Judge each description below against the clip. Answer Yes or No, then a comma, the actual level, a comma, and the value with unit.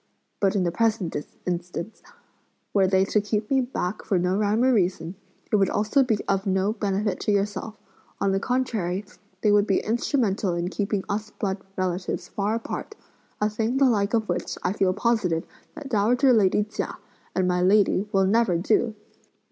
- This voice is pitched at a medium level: No, high, 205 Hz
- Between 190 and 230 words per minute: No, average, 180 wpm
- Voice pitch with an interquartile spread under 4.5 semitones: Yes, average, 2.7 semitones